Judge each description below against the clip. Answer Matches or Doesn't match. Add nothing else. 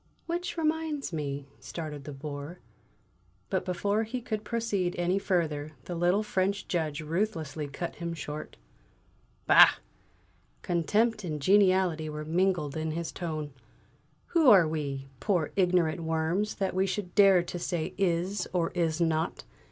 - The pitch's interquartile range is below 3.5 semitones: Doesn't match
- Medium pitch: Matches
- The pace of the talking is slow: Doesn't match